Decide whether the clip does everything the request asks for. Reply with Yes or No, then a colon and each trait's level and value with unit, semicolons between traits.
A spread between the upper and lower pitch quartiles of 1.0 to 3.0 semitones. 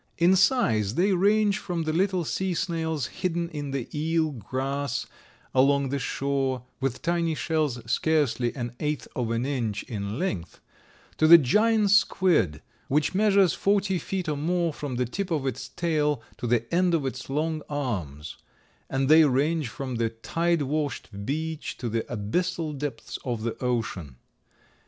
No: wide, 5.4 semitones